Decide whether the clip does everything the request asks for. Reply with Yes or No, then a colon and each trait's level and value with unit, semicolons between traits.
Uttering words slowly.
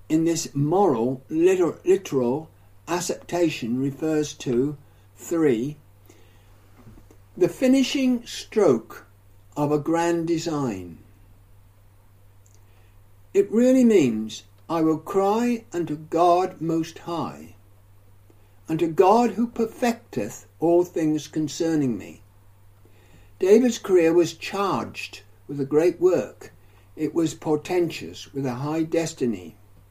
Yes: slow, 100 wpm